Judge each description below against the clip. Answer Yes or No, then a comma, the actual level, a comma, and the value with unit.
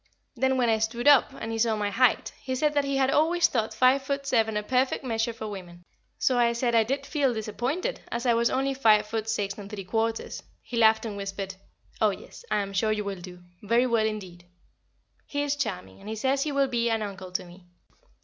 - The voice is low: No, high, 225 Hz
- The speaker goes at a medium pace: No, fast, 230 wpm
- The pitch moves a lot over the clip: No, average, 4.0 semitones